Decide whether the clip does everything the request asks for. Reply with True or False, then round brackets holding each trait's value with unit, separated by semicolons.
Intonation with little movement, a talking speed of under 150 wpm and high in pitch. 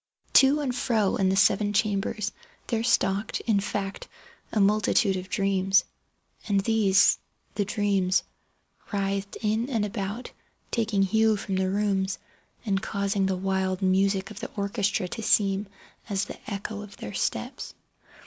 True (1.8 semitones; 140 wpm; 200 Hz)